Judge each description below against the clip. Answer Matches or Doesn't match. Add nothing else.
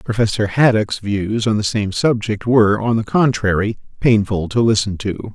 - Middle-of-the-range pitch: Doesn't match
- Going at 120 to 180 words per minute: Matches